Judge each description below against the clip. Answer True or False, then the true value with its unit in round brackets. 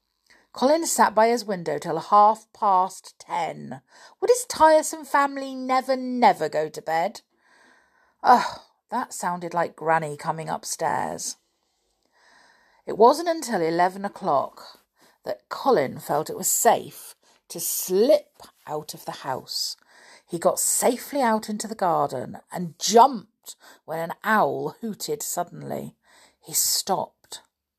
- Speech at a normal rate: False (125 wpm)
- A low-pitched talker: False (210 Hz)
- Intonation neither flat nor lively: False (8.3 semitones)